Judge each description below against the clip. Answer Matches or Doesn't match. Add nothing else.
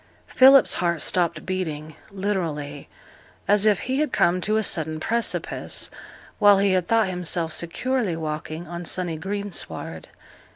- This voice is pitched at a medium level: Matches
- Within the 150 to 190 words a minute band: Doesn't match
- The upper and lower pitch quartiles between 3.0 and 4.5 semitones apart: Matches